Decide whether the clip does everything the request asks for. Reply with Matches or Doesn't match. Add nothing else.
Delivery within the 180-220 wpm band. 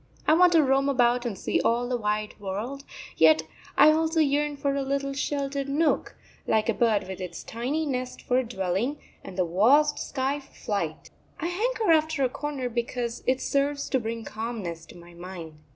Matches